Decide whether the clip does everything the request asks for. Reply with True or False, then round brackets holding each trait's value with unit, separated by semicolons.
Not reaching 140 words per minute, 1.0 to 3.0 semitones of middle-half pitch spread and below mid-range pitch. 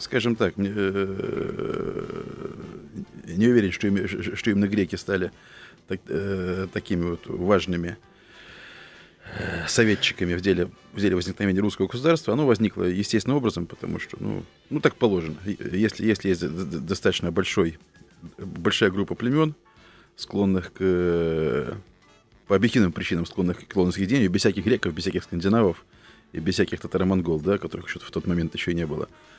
False (145 wpm; 2.7 semitones; 95 Hz)